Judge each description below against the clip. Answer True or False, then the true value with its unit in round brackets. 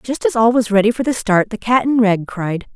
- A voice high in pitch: True (225 Hz)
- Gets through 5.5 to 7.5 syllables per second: False (5.2 syllables/s)